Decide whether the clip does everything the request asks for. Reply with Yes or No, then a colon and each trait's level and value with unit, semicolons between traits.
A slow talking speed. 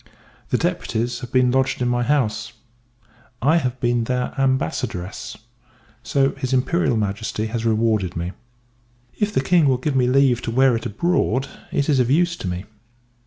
No: average, 165 wpm